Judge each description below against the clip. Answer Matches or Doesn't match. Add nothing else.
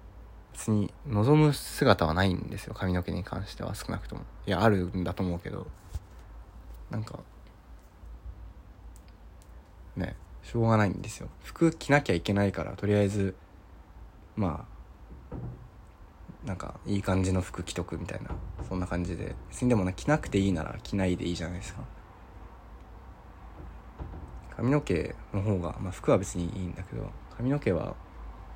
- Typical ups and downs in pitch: Matches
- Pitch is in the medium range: Doesn't match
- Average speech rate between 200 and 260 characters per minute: Doesn't match